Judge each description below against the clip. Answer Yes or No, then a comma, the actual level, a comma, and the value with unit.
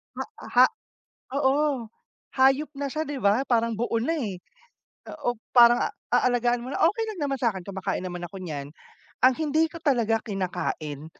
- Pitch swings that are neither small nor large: No, wide, 6.0 semitones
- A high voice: Yes, high, 240 Hz